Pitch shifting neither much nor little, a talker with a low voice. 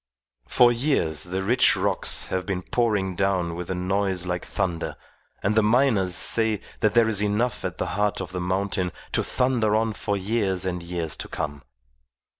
Yes: average, 3.4 semitones; very low, 95 Hz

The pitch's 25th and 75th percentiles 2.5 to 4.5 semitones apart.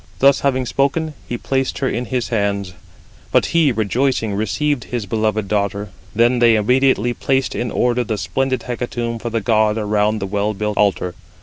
Yes: average, 3.5 semitones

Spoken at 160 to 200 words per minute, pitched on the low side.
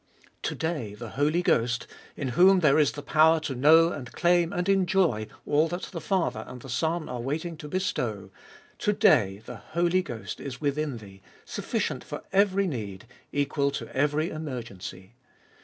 No: average, 170 wpm; medium, 150 Hz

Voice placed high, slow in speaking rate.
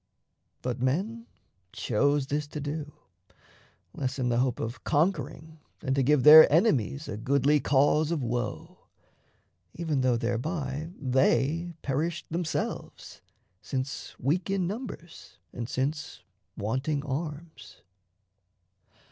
No: medium, 145 Hz; slow, 115 wpm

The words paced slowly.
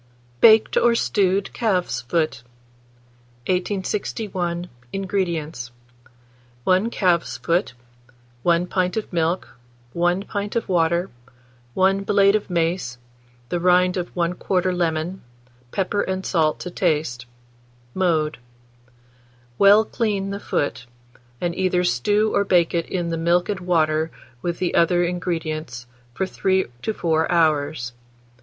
Yes: slow, 120 wpm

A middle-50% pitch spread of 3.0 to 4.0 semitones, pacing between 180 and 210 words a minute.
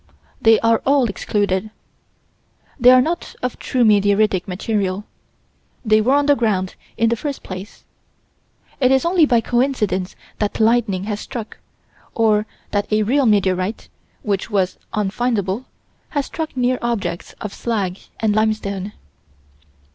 No: average, 3.6 semitones; slow, 135 wpm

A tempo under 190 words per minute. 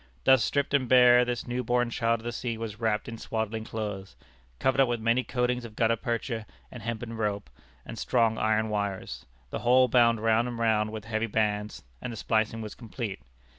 No: average, 200 wpm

